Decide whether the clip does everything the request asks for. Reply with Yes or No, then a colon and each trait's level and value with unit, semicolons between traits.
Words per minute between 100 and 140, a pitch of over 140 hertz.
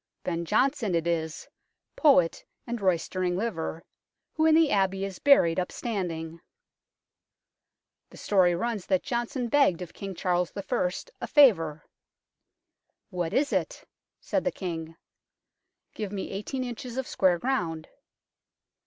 Yes: slow, 135 wpm; high, 190 Hz